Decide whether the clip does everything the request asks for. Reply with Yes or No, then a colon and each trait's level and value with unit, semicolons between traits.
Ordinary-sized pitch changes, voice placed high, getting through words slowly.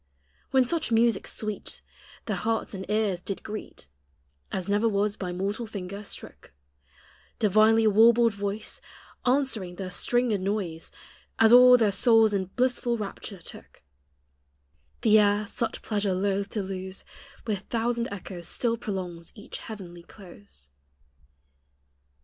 Yes: average, 3.0 semitones; high, 210 Hz; slow, 125 wpm